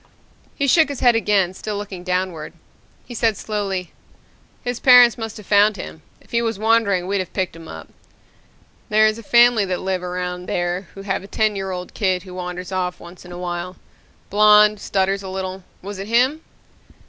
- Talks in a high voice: Yes, high, 195 Hz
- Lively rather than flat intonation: No, average, 3.0 semitones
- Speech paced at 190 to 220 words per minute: Yes, average, 195 wpm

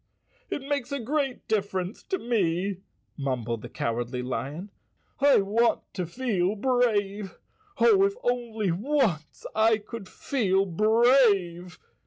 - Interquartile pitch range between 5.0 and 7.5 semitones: Yes, wide, 5.5 semitones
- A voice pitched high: Yes, high, 210 Hz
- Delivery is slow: Yes, slow, 120 wpm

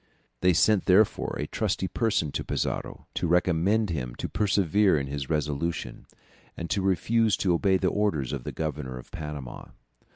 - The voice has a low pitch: Yes, very low, 85 Hz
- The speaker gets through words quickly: No, average, 165 wpm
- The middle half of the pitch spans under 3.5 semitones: No, average, 4.9 semitones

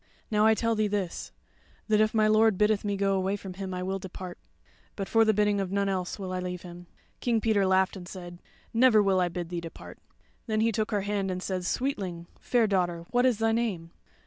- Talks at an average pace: No, fast, 225 wpm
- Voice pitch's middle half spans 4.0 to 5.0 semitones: No, average, 2.9 semitones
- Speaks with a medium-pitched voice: No, high, 195 Hz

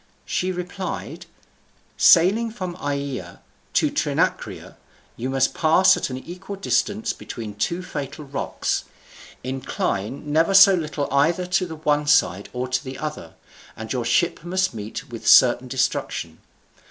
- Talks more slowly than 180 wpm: Yes, slow, 135 wpm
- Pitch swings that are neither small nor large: No, wide, 5.8 semitones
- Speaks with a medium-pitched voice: Yes, medium, 145 Hz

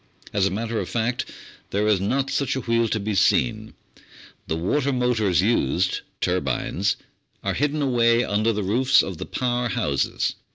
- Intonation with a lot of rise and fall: No, average, 3.9 semitones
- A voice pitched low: Yes, low, 115 Hz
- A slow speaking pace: No, average, 165 wpm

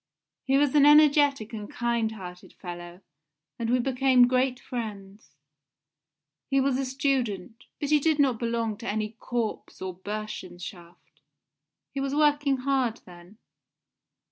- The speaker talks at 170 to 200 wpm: No, slow, 135 wpm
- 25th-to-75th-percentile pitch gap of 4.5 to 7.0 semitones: Yes, average, 4.8 semitones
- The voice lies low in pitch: No, high, 240 Hz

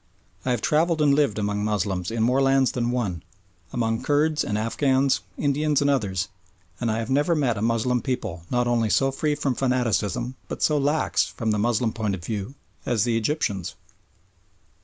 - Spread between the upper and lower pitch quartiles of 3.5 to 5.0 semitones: Yes, average, 4.4 semitones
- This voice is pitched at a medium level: No, low, 120 Hz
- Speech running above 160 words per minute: Yes, average, 180 wpm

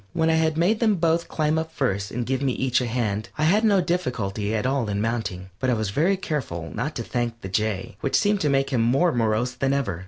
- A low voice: Yes, low, 130 Hz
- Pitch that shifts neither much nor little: No, wide, 6.5 semitones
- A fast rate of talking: Yes, fast, 250 wpm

